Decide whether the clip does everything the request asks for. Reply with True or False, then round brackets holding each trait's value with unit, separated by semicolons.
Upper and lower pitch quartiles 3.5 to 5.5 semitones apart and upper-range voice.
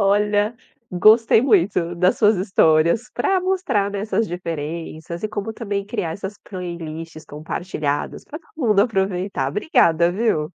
True (4.2 semitones; 195 Hz)